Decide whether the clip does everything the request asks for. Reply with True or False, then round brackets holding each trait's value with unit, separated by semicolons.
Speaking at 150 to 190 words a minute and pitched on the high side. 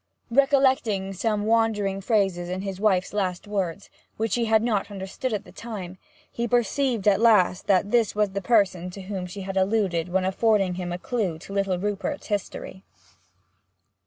True (170 wpm; 200 Hz)